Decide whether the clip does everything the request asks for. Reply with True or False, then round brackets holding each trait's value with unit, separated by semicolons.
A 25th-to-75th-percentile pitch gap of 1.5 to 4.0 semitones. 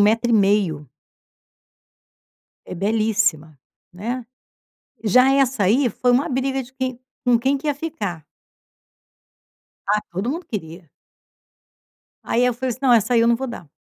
False (4.4 semitones)